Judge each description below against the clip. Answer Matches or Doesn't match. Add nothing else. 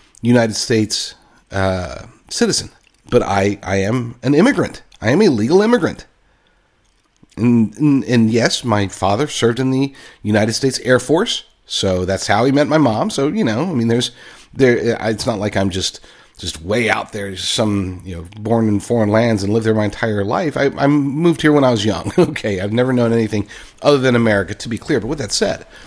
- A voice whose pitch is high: Doesn't match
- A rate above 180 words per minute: Matches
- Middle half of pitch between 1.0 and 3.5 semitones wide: Doesn't match